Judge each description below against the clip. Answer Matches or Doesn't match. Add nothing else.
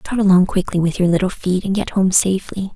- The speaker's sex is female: Matches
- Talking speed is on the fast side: Matches